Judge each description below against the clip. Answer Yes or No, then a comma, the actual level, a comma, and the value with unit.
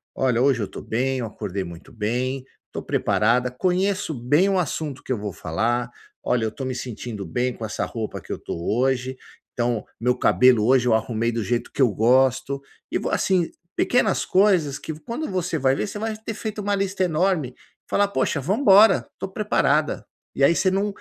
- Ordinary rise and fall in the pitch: No, wide, 7.8 semitones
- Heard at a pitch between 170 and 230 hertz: No, low, 130 Hz